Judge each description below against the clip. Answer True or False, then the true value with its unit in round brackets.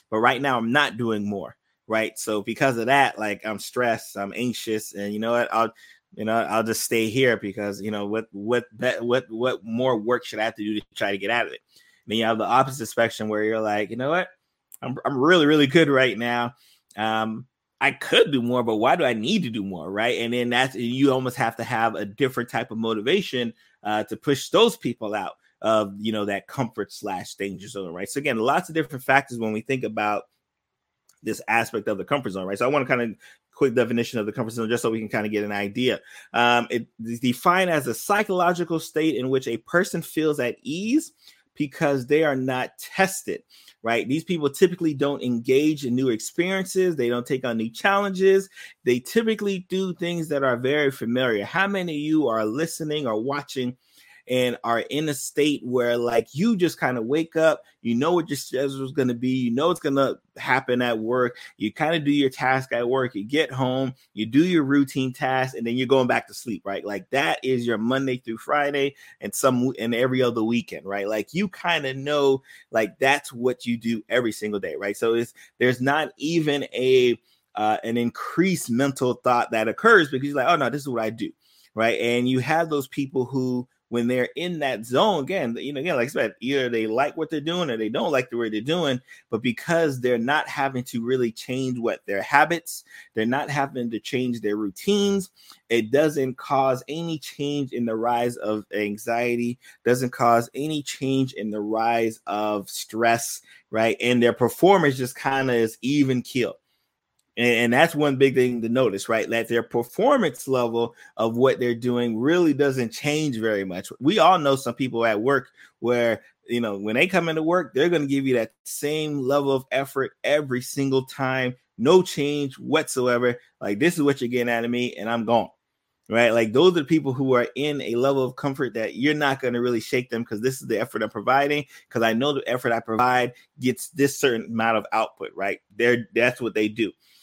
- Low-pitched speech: True (125 Hz)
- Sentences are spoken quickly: True (215 wpm)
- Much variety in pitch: False (3.8 semitones)